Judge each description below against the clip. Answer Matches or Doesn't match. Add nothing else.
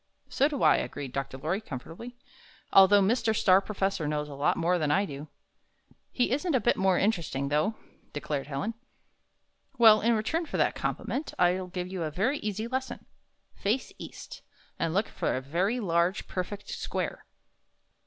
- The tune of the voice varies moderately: Doesn't match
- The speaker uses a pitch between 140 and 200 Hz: Matches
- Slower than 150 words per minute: Doesn't match